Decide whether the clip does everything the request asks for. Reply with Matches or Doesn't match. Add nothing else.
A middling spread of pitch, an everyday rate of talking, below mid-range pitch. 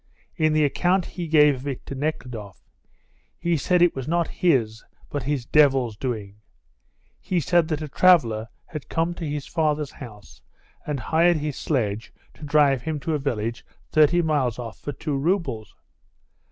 Doesn't match